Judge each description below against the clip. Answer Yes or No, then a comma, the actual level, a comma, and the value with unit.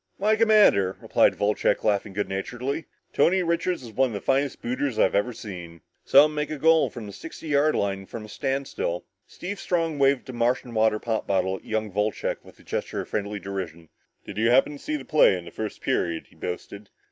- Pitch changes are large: Yes, wide, 6.5 semitones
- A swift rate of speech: Yes, fast, 215 wpm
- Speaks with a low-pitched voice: Yes, low, 115 Hz